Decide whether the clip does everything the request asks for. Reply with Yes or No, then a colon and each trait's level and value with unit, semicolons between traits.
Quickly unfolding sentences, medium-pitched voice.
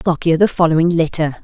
No: average, 170 wpm; medium, 165 Hz